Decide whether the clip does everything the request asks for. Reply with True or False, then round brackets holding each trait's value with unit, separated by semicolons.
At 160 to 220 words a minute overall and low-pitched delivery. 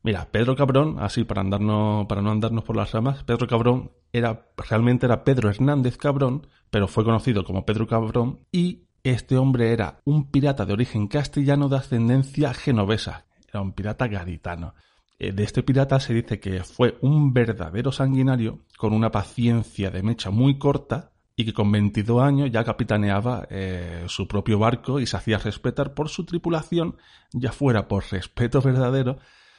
True (170 wpm; 115 Hz)